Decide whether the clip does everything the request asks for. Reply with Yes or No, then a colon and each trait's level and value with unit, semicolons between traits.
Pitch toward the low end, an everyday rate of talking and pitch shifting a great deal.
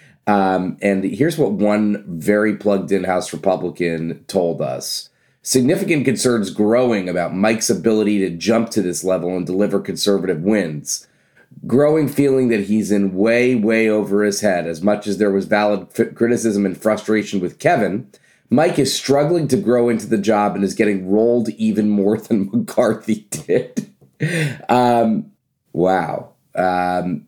No: low, 105 Hz; average, 150 wpm; average, 3.1 semitones